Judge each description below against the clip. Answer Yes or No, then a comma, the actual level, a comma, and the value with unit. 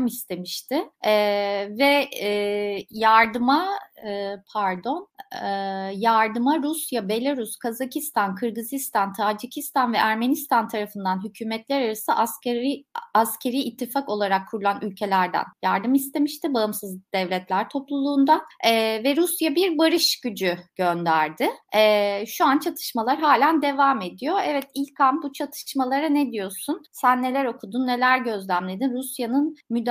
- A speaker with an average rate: Yes, average, 115 wpm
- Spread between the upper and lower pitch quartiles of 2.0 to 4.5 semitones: No, average, 5.3 semitones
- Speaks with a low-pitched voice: No, high, 240 Hz